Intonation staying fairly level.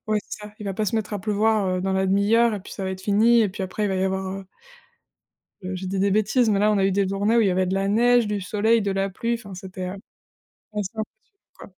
Yes: narrow, 2.2 semitones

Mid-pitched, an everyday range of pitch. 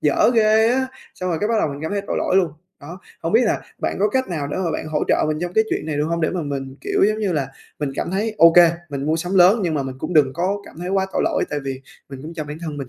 Yes: medium, 170 Hz; average, 4.6 semitones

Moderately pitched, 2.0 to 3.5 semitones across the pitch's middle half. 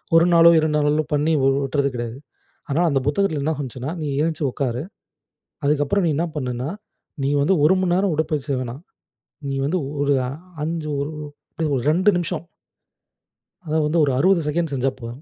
Yes: medium, 150 Hz; average, 3.1 semitones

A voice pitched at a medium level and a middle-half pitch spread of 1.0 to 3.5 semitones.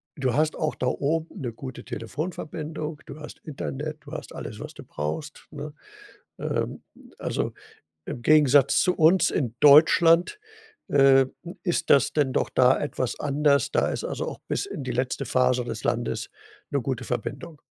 Yes: medium, 145 Hz; average, 3.1 semitones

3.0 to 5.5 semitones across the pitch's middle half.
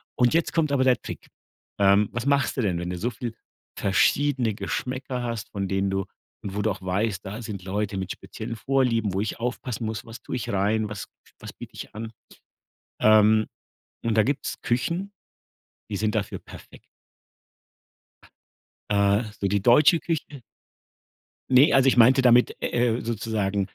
Yes: average, 3.8 semitones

